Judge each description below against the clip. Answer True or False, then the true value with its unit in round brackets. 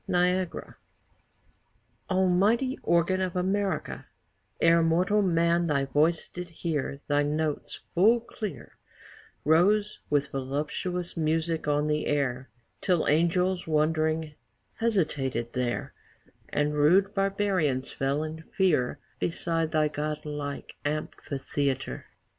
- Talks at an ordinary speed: False (105 wpm)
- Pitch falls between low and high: True (160 Hz)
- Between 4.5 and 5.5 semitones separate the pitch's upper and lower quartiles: False (3.7 semitones)